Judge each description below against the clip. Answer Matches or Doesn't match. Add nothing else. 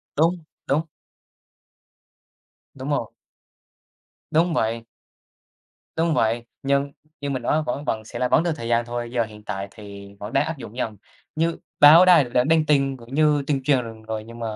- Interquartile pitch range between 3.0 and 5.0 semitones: Matches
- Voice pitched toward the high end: Doesn't match